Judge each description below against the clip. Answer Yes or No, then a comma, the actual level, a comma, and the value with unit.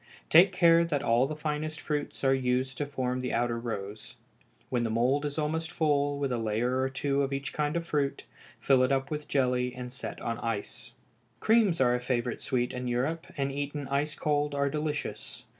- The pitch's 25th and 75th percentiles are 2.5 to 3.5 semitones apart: Yes, average, 3.1 semitones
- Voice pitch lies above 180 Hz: No, low, 135 Hz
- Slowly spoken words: No, average, 200 wpm